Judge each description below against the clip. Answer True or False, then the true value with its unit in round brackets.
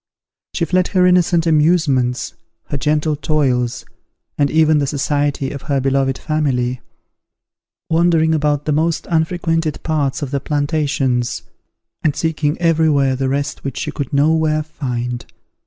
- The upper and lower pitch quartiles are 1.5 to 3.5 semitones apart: True (2.8 semitones)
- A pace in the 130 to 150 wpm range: True (140 wpm)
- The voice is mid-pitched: True (150 Hz)